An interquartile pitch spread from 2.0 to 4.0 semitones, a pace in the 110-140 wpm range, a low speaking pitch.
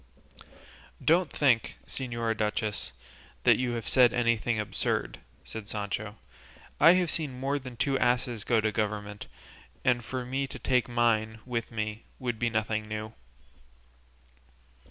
Yes: average, 2.8 semitones; slow, 135 wpm; low, 115 Hz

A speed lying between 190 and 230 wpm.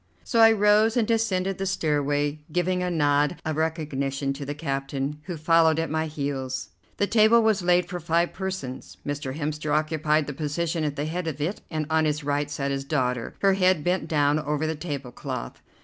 Yes: average, 195 wpm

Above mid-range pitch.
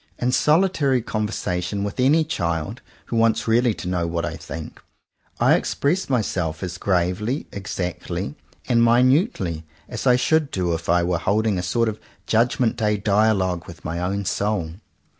No: low, 105 Hz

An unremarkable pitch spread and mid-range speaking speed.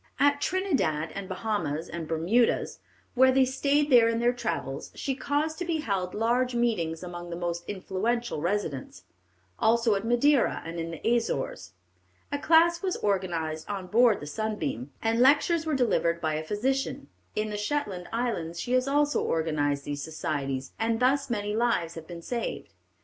No: wide, 7.3 semitones; average, 165 wpm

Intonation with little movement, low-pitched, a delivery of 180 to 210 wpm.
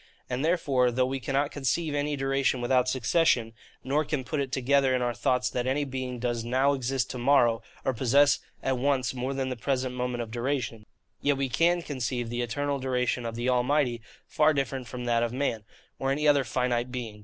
Yes: narrow, 2.3 semitones; low, 130 Hz; average, 200 wpm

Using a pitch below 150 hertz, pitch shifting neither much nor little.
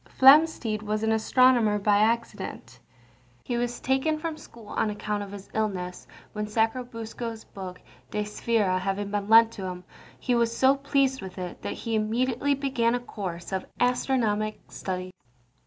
No: high, 220 Hz; average, 3.3 semitones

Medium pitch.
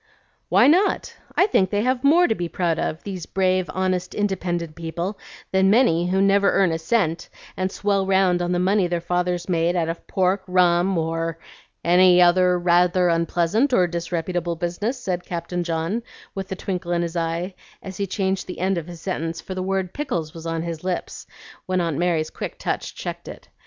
Yes: medium, 180 Hz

